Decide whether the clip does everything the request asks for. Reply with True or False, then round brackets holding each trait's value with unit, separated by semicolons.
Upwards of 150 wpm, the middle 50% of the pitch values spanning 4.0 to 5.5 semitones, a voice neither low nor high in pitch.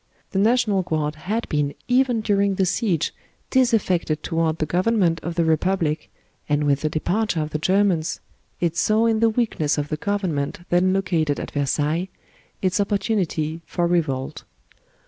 True (160 wpm; 4.7 semitones; 175 Hz)